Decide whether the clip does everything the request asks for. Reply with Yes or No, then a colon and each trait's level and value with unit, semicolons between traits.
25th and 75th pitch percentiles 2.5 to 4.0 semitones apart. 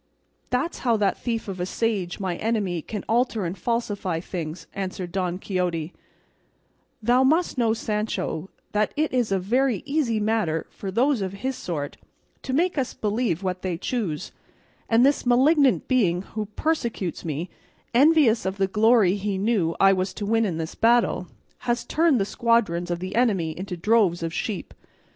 No: average, 4.7 semitones